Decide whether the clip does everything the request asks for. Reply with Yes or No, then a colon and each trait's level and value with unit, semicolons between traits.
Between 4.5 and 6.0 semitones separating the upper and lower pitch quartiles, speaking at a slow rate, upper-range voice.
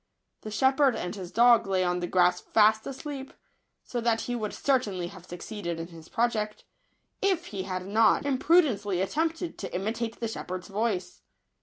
No: average, 4.9 semitones; average, 170 wpm; high, 215 Hz